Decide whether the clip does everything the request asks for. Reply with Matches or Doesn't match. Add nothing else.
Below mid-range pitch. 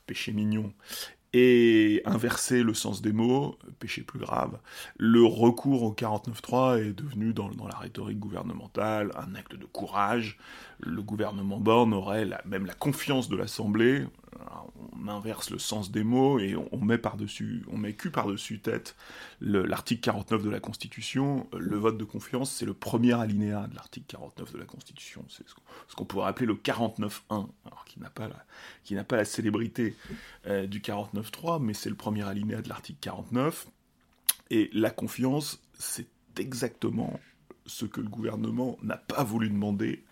Matches